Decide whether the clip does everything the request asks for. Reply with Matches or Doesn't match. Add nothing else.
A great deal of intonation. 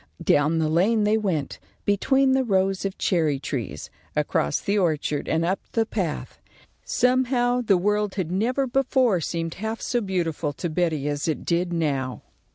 Matches